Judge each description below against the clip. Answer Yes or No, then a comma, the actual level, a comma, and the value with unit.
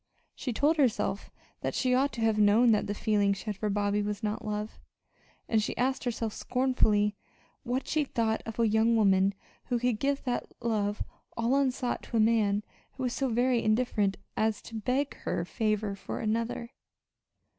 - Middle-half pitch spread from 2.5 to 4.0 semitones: Yes, average, 3.0 semitones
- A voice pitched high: Yes, high, 225 Hz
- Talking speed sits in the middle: Yes, average, 180 wpm